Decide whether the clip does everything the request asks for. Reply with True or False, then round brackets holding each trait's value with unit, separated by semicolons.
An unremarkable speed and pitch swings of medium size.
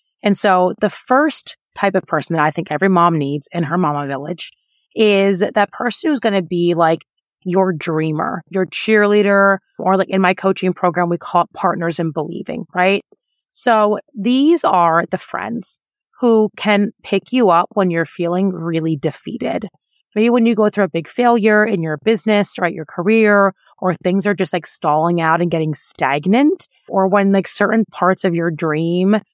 True (180 wpm; 3.7 semitones)